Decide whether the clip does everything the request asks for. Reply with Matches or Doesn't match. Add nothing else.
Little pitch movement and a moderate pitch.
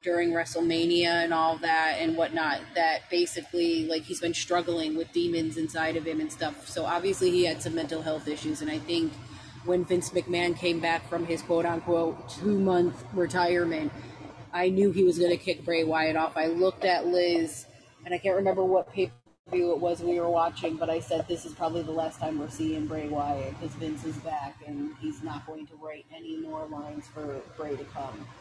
Matches